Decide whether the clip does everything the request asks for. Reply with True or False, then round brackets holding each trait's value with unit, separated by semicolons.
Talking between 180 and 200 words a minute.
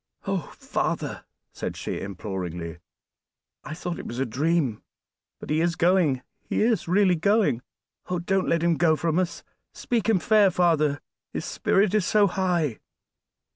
False (155 wpm)